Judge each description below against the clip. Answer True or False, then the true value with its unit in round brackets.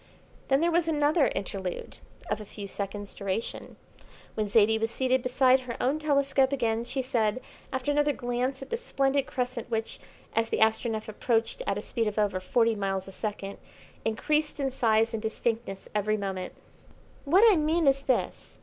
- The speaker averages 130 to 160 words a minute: False (175 wpm)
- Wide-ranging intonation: False (4.2 semitones)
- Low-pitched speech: False (235 Hz)